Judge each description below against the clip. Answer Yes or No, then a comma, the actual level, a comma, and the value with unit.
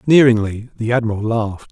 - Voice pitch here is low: Yes, low, 115 Hz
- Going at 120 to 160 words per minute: Yes, average, 140 wpm